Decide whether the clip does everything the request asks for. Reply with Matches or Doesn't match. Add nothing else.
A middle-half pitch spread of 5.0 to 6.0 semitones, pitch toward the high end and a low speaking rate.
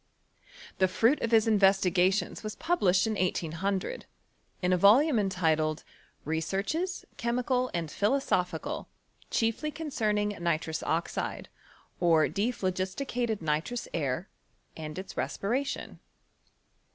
Matches